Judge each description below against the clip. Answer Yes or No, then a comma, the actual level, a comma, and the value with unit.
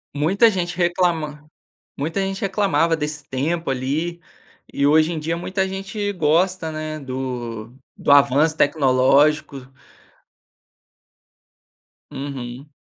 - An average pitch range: Yes, average, 3.9 semitones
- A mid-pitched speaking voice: Yes, medium, 155 Hz